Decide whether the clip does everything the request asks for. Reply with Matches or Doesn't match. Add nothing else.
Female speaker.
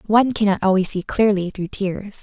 Matches